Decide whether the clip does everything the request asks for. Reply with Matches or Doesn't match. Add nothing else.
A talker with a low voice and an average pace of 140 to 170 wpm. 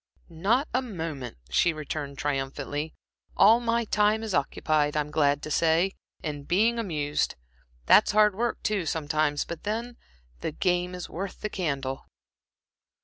Doesn't match